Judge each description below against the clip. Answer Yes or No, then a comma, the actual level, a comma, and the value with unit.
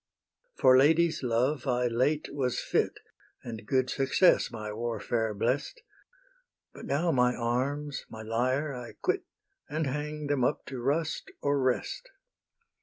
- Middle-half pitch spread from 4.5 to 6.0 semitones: No, average, 3.5 semitones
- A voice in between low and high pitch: No, low, 130 Hz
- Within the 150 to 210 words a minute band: No, slow, 135 wpm